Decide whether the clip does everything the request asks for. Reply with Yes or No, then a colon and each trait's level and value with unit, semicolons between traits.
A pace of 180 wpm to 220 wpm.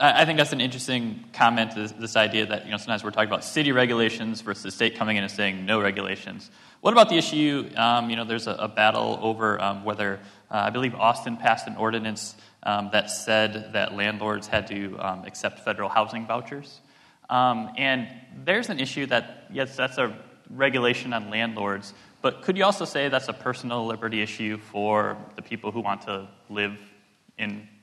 Yes: average, 195 wpm